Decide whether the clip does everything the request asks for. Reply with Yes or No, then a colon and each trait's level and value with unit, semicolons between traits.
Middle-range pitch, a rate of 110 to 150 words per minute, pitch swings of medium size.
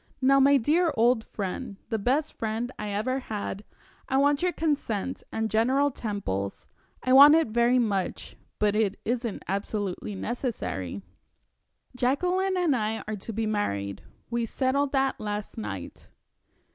No: high, 230 Hz; average, 145 wpm; average, 4.6 semitones